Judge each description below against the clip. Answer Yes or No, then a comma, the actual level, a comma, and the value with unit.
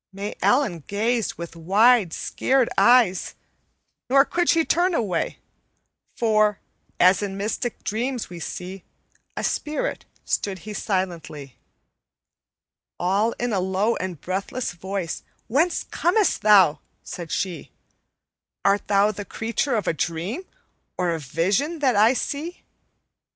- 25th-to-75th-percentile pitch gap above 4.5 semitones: Yes, average, 5.1 semitones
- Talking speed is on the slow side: Yes, slow, 125 wpm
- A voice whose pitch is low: No, high, 205 Hz